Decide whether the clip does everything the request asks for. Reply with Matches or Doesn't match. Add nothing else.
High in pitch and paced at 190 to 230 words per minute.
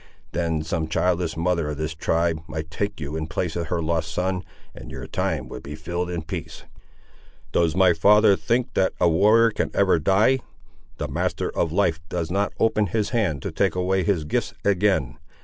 Doesn't match